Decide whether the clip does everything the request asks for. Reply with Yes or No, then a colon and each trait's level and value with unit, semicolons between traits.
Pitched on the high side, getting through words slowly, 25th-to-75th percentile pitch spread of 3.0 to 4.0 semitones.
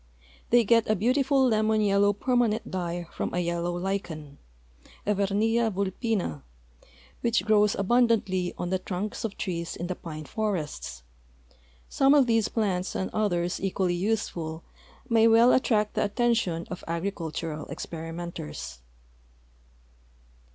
No: high, 195 Hz; slow, 125 wpm; average, 4.5 semitones